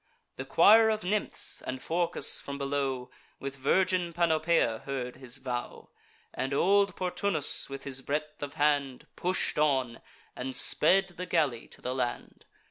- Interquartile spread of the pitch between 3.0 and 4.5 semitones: No, average, 5.1 semitones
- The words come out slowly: No, average, 145 wpm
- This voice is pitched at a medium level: Yes, medium, 145 Hz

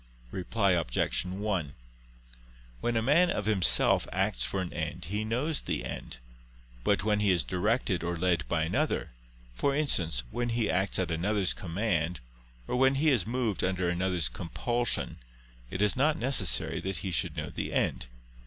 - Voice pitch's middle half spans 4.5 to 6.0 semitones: Yes, average, 4.9 semitones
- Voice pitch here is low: Yes, very low, 95 Hz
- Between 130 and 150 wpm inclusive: No, average, 165 wpm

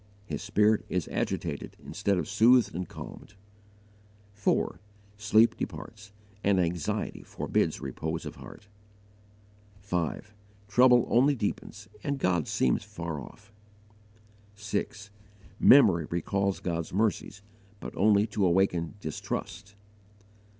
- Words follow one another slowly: Yes, slow, 110 wpm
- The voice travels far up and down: No, average, 3.3 semitones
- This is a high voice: No, low, 100 Hz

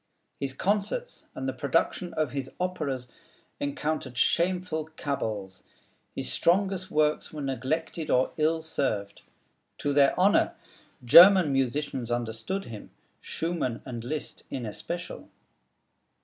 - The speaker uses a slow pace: Yes, slow, 115 wpm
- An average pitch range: Yes, average, 5.0 semitones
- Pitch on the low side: No, medium, 145 Hz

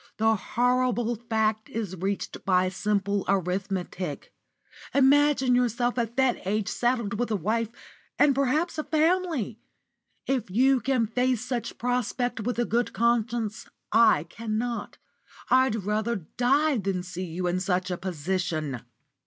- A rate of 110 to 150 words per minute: Yes, slow, 135 wpm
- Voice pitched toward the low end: No, high, 225 Hz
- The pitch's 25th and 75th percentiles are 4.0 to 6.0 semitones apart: Yes, average, 4.3 semitones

